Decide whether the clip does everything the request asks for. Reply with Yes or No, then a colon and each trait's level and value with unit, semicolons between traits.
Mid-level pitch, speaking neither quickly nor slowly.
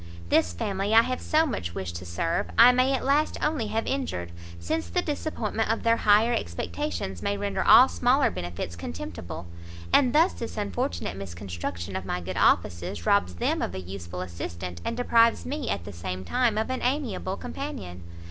No: low, 100 Hz; average, 180 wpm